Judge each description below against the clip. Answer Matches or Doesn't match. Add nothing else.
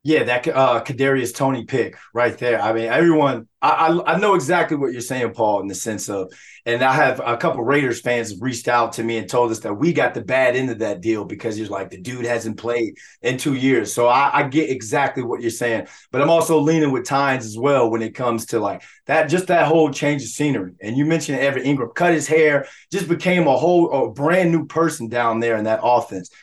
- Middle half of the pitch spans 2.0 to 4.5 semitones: Doesn't match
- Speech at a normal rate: Doesn't match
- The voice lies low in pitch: Matches